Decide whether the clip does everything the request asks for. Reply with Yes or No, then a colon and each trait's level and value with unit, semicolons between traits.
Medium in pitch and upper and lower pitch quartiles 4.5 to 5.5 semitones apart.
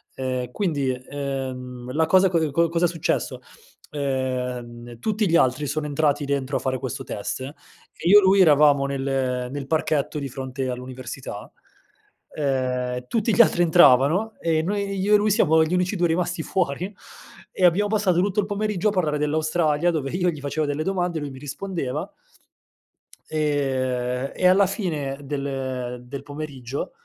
Yes: medium, 145 Hz; average, 5.1 semitones